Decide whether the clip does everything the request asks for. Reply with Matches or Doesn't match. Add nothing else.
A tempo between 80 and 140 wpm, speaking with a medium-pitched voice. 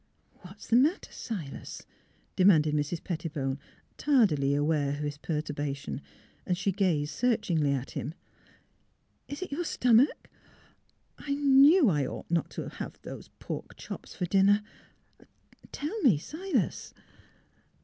Matches